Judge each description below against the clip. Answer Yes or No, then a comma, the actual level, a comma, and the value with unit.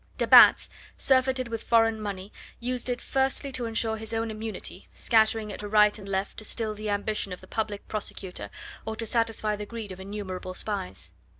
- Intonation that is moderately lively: No, narrow, 2.0 semitones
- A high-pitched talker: Yes, high, 215 Hz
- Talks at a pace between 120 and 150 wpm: No, average, 190 wpm